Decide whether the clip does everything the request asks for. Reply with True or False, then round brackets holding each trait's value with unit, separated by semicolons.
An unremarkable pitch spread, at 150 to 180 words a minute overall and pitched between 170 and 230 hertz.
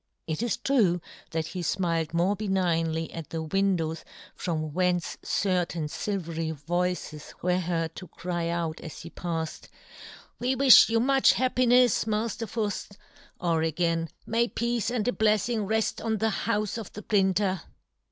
True (5.0 semitones; 160 wpm; 185 Hz)